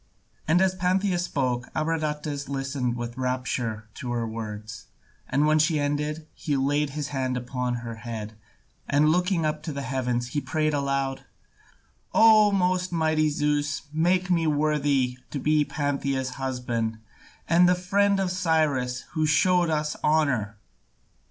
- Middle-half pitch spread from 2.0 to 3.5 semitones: No, average, 3.9 semitones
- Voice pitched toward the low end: No, medium, 145 Hz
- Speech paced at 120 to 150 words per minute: Yes, average, 140 wpm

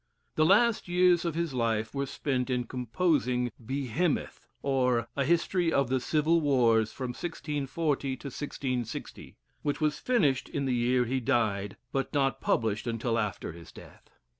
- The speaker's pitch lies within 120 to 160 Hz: Yes, low, 135 Hz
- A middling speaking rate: Yes, average, 155 wpm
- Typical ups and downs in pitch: Yes, average, 4.2 semitones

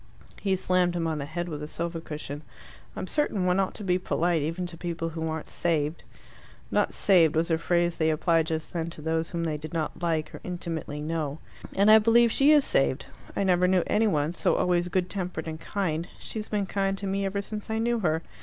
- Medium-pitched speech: Yes, medium, 175 Hz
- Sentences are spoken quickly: Yes, fast, 225 wpm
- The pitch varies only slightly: No, average, 3.2 semitones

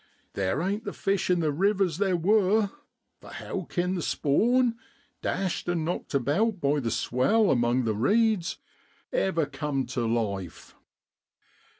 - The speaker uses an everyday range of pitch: No, wide, 6.9 semitones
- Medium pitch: Yes, medium, 175 Hz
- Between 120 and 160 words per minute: Yes, average, 140 wpm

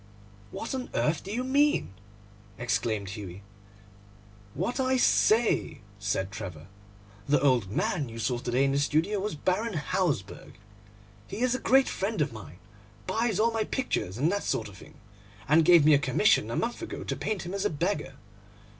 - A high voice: No, medium, 155 Hz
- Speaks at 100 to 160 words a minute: No, average, 180 wpm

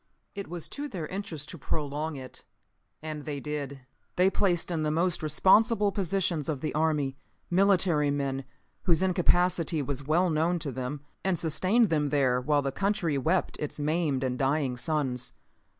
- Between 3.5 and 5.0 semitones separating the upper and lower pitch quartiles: Yes, average, 4.0 semitones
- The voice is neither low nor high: Yes, medium, 155 Hz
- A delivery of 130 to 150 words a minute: No, average, 165 wpm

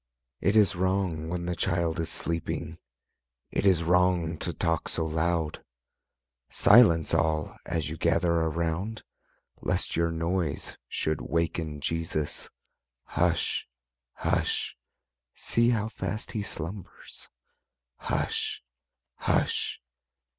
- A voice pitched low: Yes, very low, 85 Hz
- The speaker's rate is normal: No, slow, 105 wpm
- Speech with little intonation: Yes, narrow, 2.2 semitones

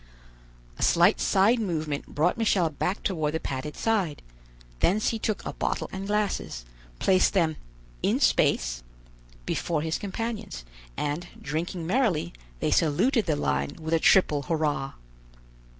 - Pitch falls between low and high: Yes, medium, 165 Hz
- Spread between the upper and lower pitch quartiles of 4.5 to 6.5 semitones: Yes, average, 5.1 semitones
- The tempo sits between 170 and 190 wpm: No, slow, 135 wpm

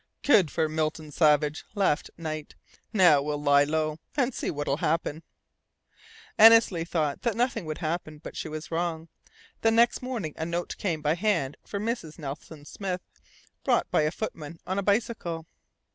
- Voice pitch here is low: No, medium, 160 Hz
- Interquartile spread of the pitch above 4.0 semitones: Yes, average, 4.6 semitones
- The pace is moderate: Yes, average, 165 wpm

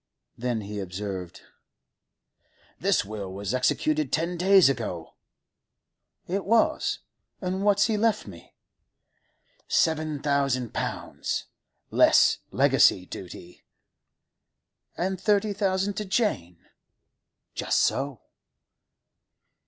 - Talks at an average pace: No, slow, 90 wpm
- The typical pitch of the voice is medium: Yes, medium, 150 Hz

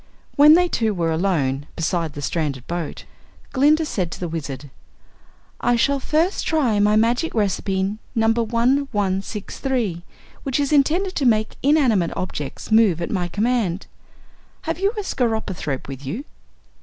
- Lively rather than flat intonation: Yes, wide, 7.8 semitones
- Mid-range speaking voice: No, high, 215 Hz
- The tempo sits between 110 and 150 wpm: Yes, average, 145 wpm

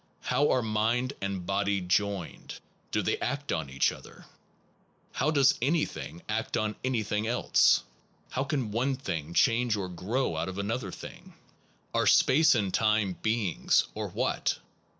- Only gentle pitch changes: No, average, 4.7 semitones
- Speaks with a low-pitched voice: Yes, low, 110 Hz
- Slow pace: No, average, 145 wpm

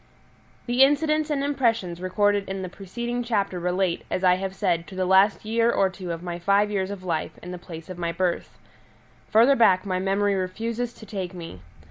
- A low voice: No, high, 195 Hz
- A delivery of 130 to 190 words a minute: No, average, 200 wpm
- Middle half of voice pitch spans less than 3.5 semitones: No, average, 3.8 semitones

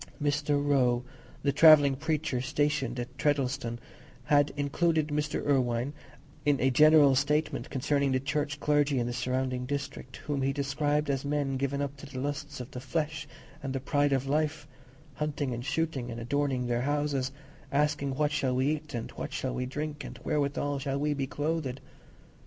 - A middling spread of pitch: No, narrow, 2.1 semitones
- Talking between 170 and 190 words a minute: Yes, average, 175 wpm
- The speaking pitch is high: No, medium, 140 Hz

